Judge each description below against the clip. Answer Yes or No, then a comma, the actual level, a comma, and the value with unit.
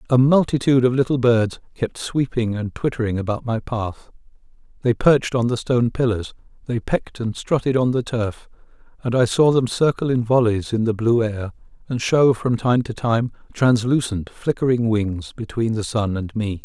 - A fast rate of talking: No, average, 180 wpm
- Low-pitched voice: Yes, low, 120 Hz